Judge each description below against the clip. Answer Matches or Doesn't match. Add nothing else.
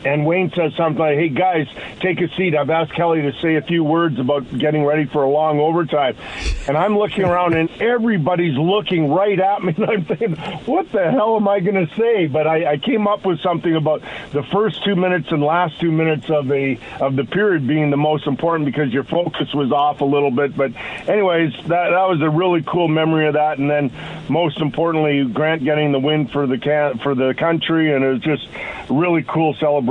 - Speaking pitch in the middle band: Matches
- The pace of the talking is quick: Matches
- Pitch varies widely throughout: Doesn't match